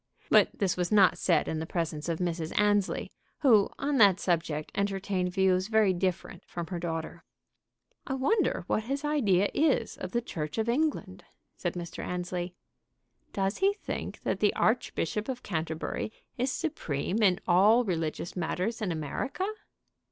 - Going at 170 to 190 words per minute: No, average, 155 wpm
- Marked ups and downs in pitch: No, average, 4.5 semitones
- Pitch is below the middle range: No, high, 190 Hz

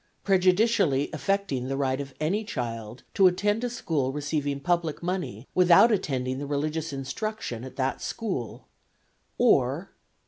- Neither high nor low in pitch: Yes, medium, 150 Hz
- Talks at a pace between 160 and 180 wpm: No, average, 140 wpm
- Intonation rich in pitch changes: Yes, wide, 5.9 semitones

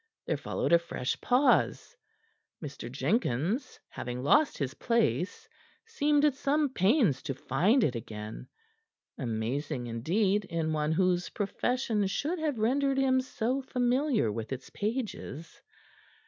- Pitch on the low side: No, high, 200 Hz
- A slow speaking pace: Yes, slow, 125 wpm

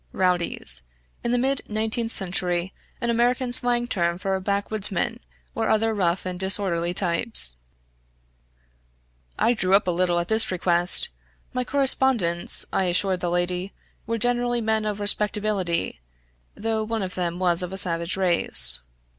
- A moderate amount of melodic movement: Yes, average, 4.2 semitones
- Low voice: No, high, 195 Hz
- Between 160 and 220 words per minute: No, average, 145 wpm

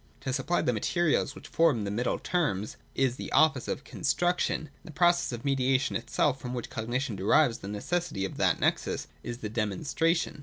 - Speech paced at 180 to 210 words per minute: Yes, average, 190 wpm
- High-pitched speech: No, low, 130 Hz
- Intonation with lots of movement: Yes, wide, 5.8 semitones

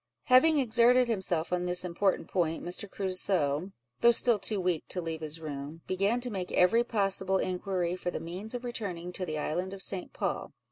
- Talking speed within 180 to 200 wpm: Yes, average, 190 wpm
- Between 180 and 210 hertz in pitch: Yes, medium, 185 Hz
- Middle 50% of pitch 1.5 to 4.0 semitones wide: Yes, average, 3.5 semitones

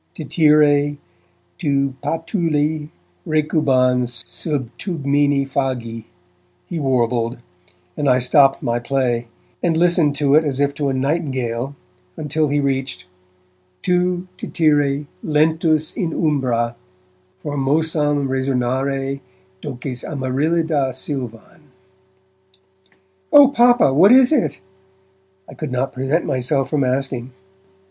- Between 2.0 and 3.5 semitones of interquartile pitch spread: Yes, average, 3.0 semitones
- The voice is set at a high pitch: No, medium, 140 Hz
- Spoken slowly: Yes, slow, 100 wpm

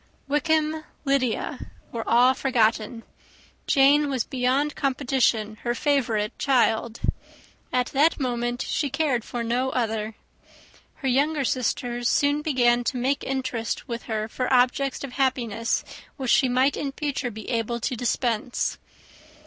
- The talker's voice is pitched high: Yes, very high, 255 Hz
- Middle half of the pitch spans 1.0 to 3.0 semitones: Yes, average, 2.7 semitones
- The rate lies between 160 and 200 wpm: No, slow, 135 wpm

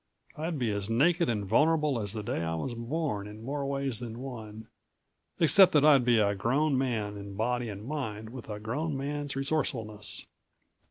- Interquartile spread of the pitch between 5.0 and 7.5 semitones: Yes, average, 5.3 semitones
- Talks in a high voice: No, low, 120 Hz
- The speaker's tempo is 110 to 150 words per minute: No, average, 180 wpm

